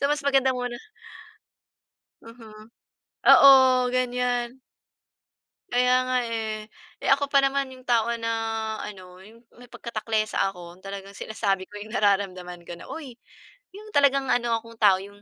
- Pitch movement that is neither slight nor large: Yes, average, 3.9 semitones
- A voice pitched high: Yes, high, 230 Hz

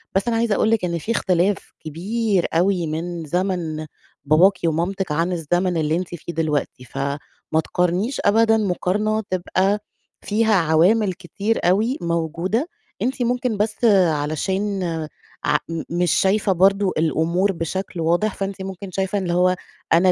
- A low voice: No, medium, 185 Hz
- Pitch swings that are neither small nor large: Yes, average, 3.5 semitones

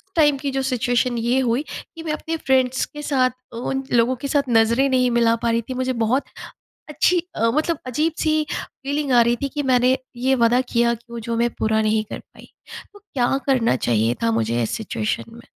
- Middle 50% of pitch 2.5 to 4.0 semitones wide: Yes, average, 3.0 semitones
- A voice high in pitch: Yes, very high, 250 Hz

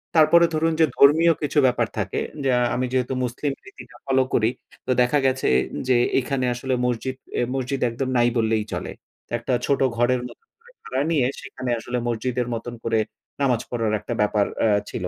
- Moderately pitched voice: No, low, 130 Hz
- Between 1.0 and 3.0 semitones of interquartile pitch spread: Yes, narrow, 2.6 semitones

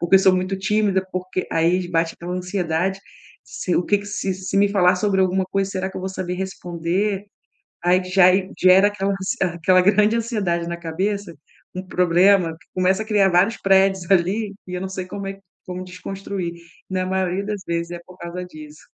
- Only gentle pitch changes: Yes, narrow, 1.6 semitones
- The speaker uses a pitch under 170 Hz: No, medium, 185 Hz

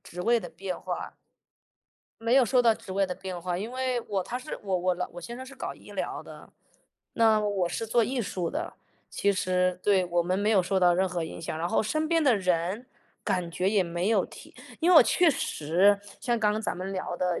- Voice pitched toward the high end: Yes, high, 195 Hz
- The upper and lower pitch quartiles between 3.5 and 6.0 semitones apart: Yes, average, 4.4 semitones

